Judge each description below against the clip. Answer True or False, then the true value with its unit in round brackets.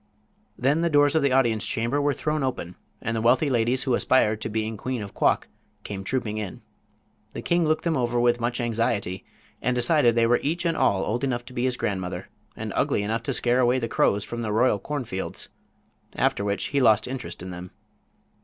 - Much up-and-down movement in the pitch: False (3.4 semitones)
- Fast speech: True (210 wpm)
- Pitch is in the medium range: False (120 Hz)